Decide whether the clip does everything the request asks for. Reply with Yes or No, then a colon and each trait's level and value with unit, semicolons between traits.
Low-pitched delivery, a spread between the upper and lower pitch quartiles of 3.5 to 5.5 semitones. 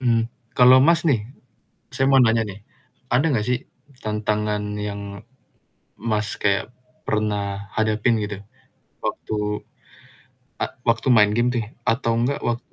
No: low, 110 Hz; average, 2.7 semitones